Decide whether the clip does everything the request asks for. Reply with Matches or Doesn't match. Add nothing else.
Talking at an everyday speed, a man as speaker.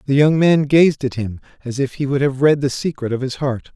Doesn't match